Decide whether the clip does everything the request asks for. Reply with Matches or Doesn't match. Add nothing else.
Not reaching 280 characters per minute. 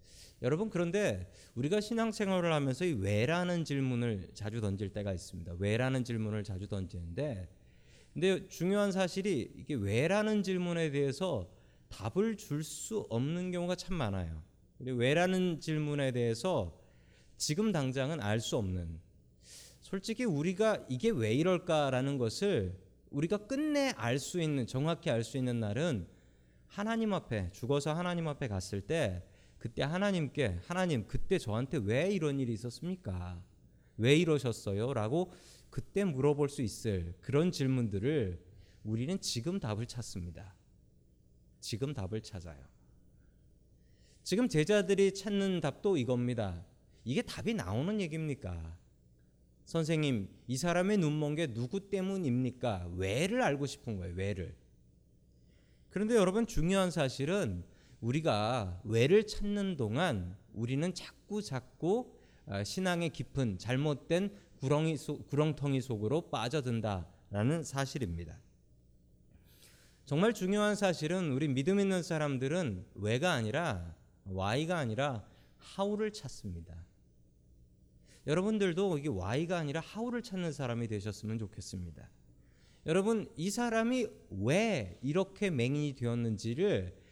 Doesn't match